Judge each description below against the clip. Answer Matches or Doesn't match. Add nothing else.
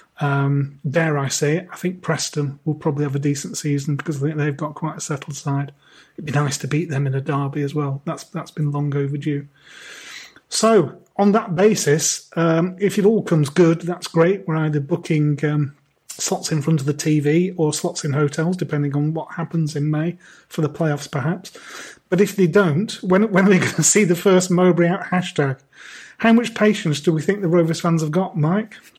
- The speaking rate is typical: Doesn't match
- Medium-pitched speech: Matches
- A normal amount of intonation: Matches